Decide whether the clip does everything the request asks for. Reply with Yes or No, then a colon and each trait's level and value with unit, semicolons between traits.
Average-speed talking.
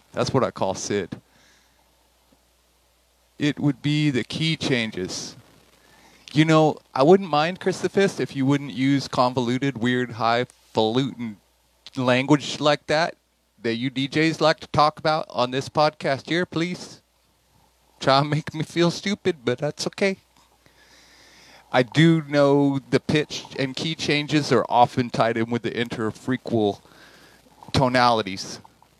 No: slow, 130 wpm